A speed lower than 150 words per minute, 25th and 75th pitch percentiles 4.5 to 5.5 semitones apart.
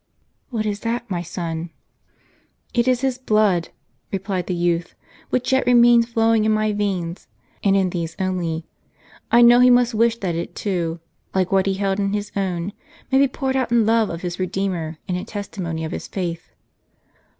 No: average, 190 wpm; average, 4.8 semitones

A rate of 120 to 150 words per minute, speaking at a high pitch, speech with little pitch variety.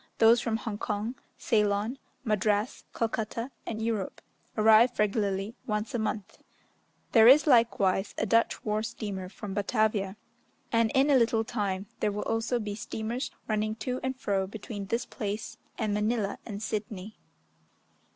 Yes: average, 145 wpm; high, 215 Hz; narrow, 2.0 semitones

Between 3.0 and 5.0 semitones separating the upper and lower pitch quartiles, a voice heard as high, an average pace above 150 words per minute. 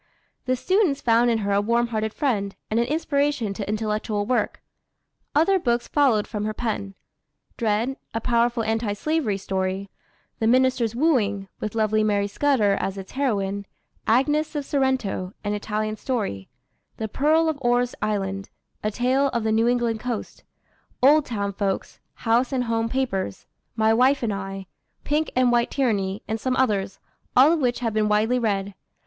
Yes: average, 3.9 semitones; high, 225 Hz; average, 165 wpm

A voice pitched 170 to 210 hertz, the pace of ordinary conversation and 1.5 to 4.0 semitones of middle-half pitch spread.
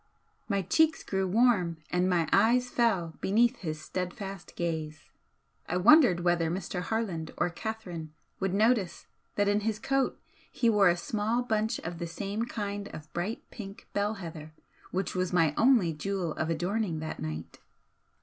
No: high, 190 Hz; average, 160 wpm; average, 4.4 semitones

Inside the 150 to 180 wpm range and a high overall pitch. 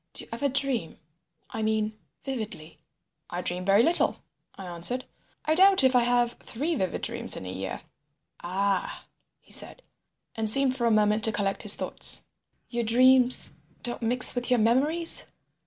Yes: average, 165 wpm; high, 235 Hz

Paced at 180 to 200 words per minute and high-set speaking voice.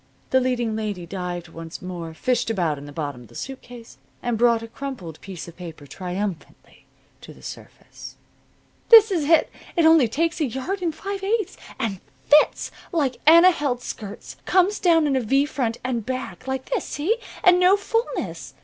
Yes: average, 185 wpm; very high, 250 Hz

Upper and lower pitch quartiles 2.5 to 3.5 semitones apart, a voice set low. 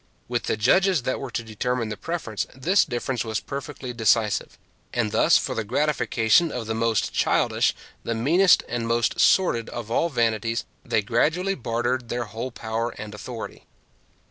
Yes: average, 2.8 semitones; low, 120 Hz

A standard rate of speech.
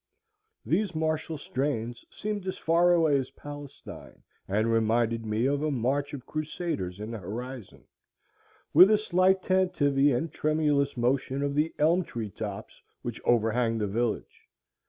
Yes: average, 145 wpm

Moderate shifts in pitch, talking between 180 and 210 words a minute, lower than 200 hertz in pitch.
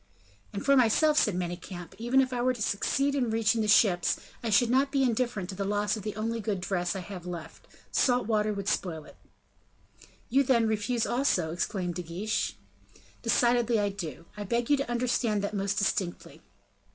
No: average, 4.0 semitones; average, 190 wpm; high, 215 Hz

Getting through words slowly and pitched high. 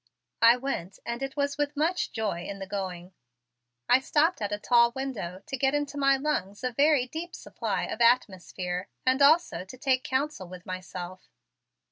No: average, 175 wpm; very high, 250 Hz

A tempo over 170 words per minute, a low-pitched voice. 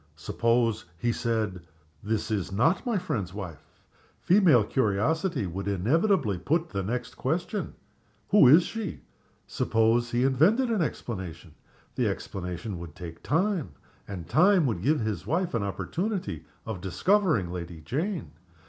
No: slow, 135 wpm; low, 115 Hz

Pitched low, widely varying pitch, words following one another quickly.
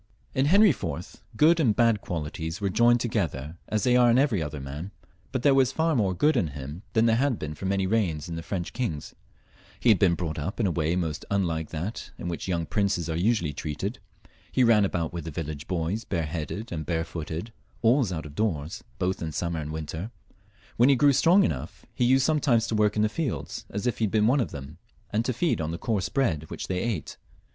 Yes: very low, 95 Hz; wide, 6.6 semitones; fast, 225 wpm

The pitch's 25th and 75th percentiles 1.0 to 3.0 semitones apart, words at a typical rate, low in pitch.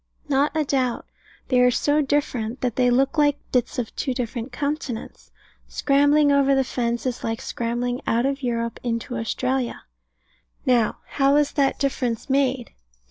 No: narrow, 2.6 semitones; average, 155 wpm; very high, 255 Hz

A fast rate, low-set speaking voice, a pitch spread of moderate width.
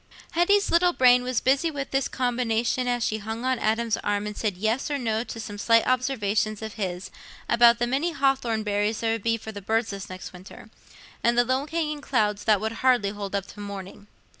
No: fast, 215 wpm; high, 230 Hz; average, 3.6 semitones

